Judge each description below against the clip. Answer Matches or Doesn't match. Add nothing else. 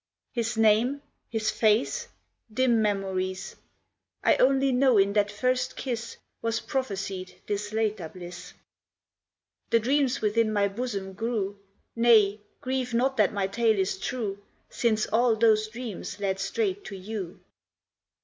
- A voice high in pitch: Matches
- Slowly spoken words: Matches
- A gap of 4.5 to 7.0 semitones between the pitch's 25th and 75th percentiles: Doesn't match